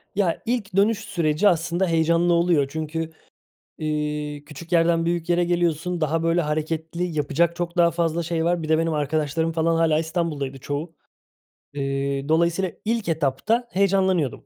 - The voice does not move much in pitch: Yes, narrow, 2.2 semitones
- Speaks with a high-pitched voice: No, medium, 165 Hz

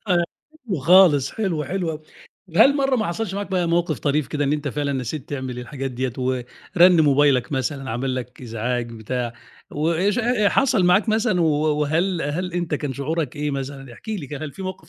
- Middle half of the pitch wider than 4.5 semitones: Yes, average, 5.1 semitones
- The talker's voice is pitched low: No, medium, 150 Hz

